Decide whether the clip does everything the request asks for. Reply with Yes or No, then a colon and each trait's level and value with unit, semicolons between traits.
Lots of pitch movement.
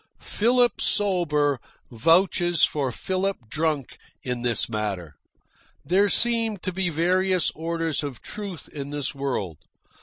Yes: wide, 5.7 semitones